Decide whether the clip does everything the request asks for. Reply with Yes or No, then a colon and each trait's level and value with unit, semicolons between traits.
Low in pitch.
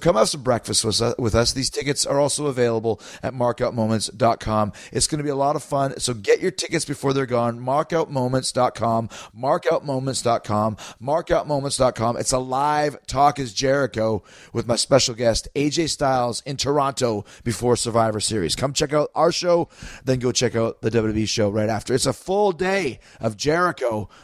Yes: low, 130 Hz